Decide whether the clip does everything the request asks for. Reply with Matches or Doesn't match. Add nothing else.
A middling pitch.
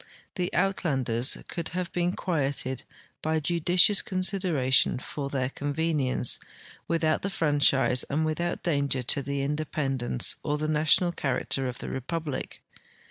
Matches